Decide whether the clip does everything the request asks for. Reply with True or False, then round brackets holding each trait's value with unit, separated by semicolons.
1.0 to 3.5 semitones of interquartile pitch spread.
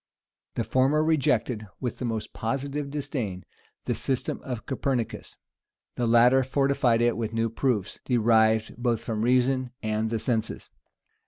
True (3.0 semitones)